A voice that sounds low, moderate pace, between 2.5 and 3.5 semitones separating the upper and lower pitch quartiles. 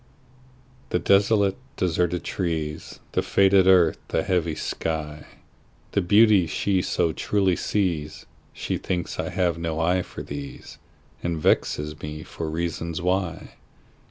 No: very low, 85 Hz; slow, 110 wpm; average, 2.9 semitones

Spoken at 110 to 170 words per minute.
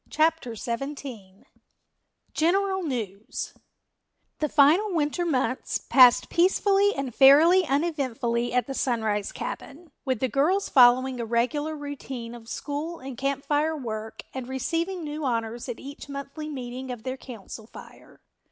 Yes: slow, 135 wpm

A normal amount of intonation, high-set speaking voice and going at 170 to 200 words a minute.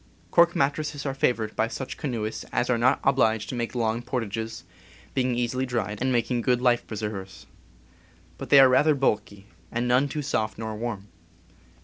No: average, 3.0 semitones; low, 120 Hz; average, 175 wpm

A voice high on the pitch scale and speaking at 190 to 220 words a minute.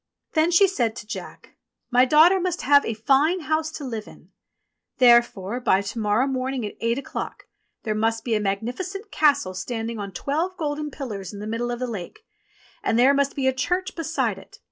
Yes: very high, 255 Hz; average, 195 wpm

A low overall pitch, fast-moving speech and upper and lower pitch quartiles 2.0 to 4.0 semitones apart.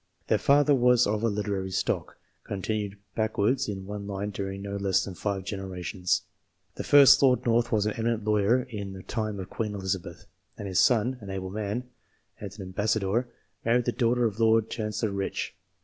No: low, 105 Hz; average, 190 wpm; average, 2.9 semitones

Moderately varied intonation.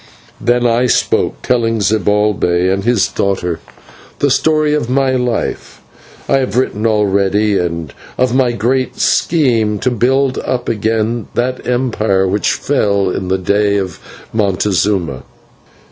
Yes: average, 4.1 semitones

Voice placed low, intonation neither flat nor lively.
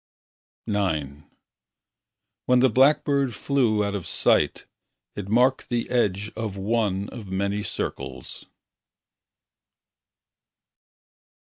Yes: low, 105 Hz; average, 3.9 semitones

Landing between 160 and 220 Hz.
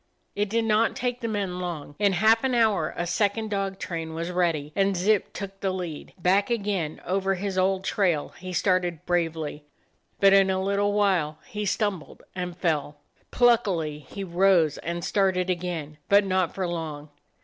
Yes: medium, 185 Hz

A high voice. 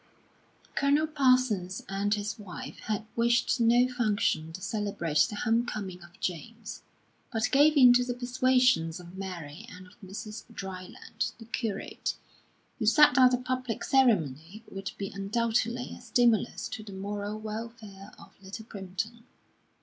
Yes: high, 215 Hz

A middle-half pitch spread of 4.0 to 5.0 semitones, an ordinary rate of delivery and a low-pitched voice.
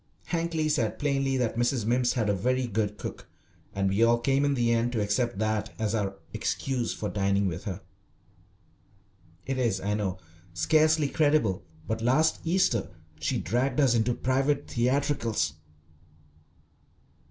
Yes: average, 4.6 semitones; average, 150 wpm; low, 120 Hz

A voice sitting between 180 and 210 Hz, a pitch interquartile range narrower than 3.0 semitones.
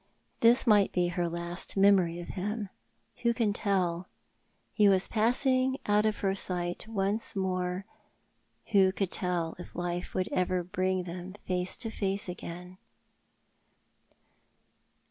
Yes: high, 190 Hz; narrow, 2.5 semitones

